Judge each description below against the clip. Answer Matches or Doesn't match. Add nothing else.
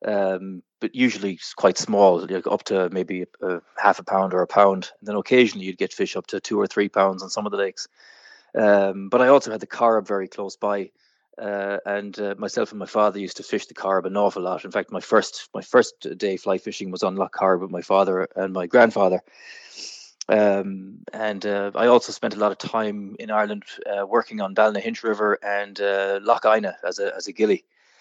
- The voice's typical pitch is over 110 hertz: Doesn't match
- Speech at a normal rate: Doesn't match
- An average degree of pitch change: Doesn't match